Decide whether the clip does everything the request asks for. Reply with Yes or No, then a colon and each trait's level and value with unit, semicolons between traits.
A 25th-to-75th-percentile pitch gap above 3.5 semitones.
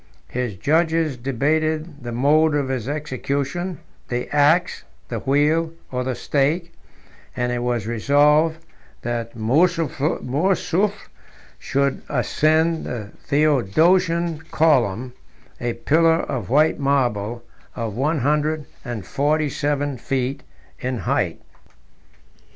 Yes: average, 4.2 semitones